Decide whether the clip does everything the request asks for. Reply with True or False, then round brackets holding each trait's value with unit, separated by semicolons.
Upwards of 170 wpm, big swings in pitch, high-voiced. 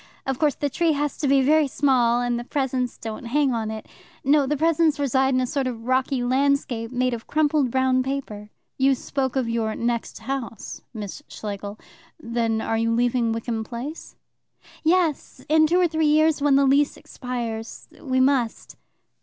False (180 wpm; 3.6 semitones; 260 Hz)